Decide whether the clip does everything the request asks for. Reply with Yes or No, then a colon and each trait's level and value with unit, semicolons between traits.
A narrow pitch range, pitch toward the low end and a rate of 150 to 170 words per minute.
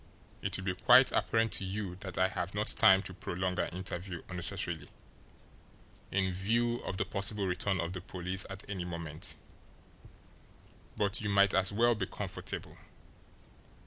Yes: narrow, 2.0 semitones; very low, 95 Hz; average, 155 wpm